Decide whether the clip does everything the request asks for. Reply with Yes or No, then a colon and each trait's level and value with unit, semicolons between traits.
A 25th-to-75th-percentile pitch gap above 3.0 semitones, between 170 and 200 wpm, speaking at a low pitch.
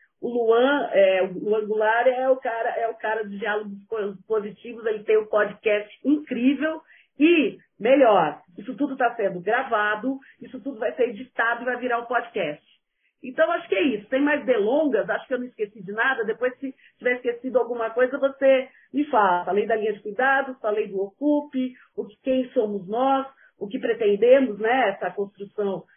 No: average, 4.0 semitones; fast, 185 wpm; high, 240 Hz